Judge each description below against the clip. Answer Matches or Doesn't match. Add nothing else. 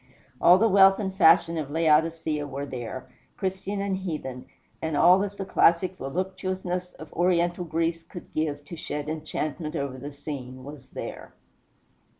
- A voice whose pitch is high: Doesn't match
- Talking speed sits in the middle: Matches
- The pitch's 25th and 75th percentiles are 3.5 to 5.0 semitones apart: Matches